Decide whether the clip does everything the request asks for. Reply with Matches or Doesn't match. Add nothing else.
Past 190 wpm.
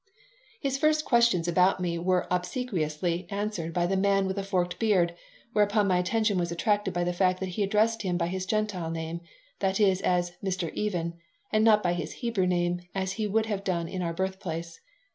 Matches